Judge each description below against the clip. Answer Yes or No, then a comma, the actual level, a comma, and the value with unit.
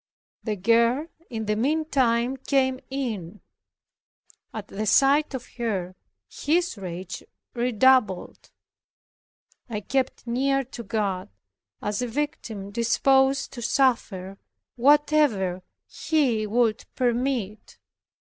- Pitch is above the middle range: Yes, high, 235 Hz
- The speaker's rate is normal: No, slow, 100 wpm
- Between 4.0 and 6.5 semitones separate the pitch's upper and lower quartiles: Yes, average, 4.3 semitones